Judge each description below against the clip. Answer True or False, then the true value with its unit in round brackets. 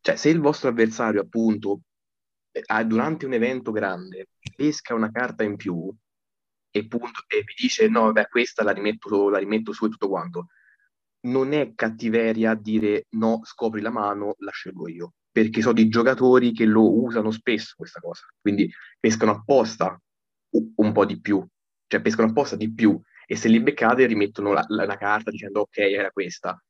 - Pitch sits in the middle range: False (110 Hz)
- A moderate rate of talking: False (175 wpm)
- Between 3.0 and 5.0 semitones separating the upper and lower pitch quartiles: False (2.6 semitones)